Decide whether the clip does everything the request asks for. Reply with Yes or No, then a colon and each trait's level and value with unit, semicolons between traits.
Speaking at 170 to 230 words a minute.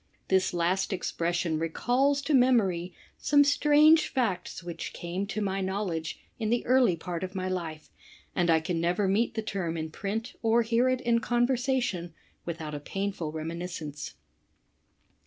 No: average, 155 wpm